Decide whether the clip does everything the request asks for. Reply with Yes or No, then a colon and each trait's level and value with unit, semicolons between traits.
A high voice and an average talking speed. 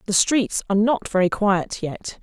Yes: high, 200 Hz; average, 190 wpm